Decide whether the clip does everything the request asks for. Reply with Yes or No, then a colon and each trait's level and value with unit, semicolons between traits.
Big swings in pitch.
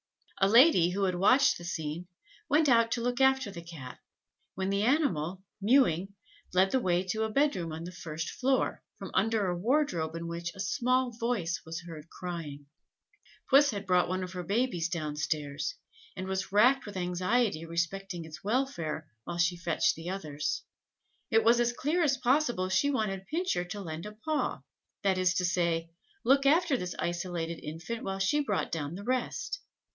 Yes: wide, 6.1 semitones